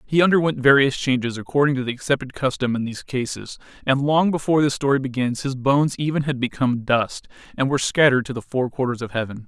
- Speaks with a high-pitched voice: No, low, 135 Hz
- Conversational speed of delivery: No, fast, 210 wpm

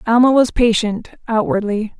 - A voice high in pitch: Yes, high, 225 Hz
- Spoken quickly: No, slow, 90 wpm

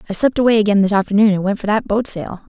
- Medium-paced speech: No, fast, 285 wpm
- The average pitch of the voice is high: Yes, high, 210 Hz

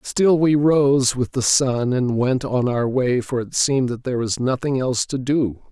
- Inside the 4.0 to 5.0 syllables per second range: Yes, 4.5 syllables/s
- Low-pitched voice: Yes, low, 130 Hz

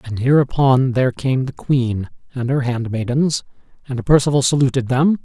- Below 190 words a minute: Yes, average, 150 wpm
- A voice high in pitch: No, low, 130 Hz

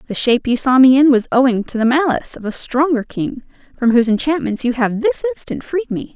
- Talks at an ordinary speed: No, fast, 235 wpm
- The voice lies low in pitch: No, very high, 255 Hz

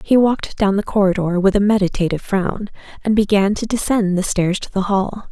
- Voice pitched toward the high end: Yes, high, 200 Hz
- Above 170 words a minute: Yes, fast, 205 wpm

